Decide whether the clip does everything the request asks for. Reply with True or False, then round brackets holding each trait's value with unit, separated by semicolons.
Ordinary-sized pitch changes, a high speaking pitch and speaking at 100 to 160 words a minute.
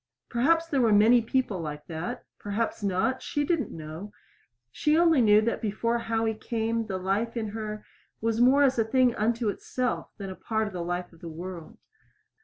False (3.7 semitones; 220 Hz; 195 wpm)